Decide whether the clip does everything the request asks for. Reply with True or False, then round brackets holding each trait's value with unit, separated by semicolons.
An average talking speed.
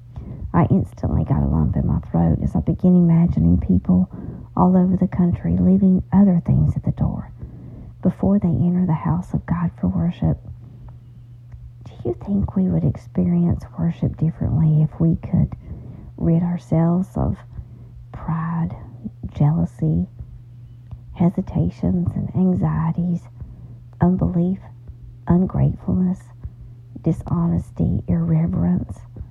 False (115 wpm)